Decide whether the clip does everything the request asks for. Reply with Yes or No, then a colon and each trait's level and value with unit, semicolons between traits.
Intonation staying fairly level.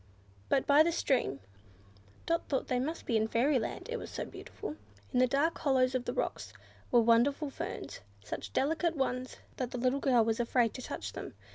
No: average, 3.1 semitones